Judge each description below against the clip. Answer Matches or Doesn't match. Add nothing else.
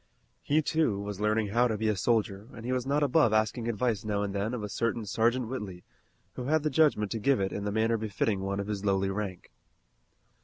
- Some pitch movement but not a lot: Matches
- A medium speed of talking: Doesn't match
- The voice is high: Doesn't match